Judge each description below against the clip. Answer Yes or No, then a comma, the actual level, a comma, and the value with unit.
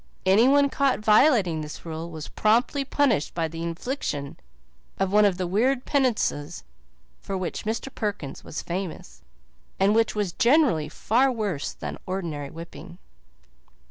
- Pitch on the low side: No, high, 195 Hz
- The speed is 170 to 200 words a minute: No, average, 140 wpm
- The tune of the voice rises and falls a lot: Yes, wide, 6.8 semitones